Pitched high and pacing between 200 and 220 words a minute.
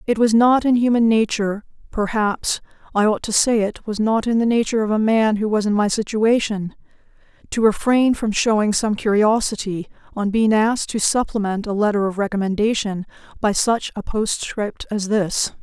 No: high, 215 Hz; average, 170 wpm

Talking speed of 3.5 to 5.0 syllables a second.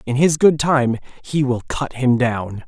Yes: 4.1 syllables/s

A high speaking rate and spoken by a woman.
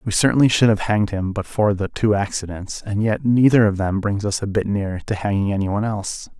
No: fast, 245 wpm; male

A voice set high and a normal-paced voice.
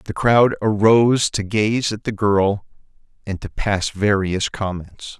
No: low, 105 Hz; average, 150 wpm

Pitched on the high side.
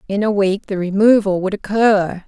Yes: high, 200 Hz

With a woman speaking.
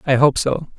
No: male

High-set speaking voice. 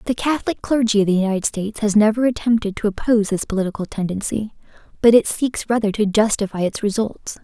Yes: high, 215 Hz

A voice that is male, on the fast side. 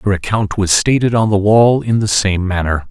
Yes: male; fast, 225 wpm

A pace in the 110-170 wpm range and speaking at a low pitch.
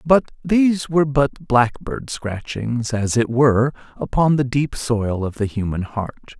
Yes: average, 160 wpm; low, 130 Hz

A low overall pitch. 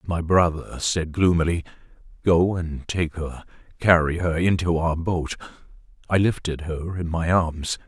Yes: very low, 85 Hz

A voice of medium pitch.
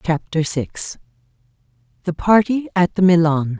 Yes: medium, 170 Hz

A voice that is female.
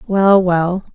Yes: female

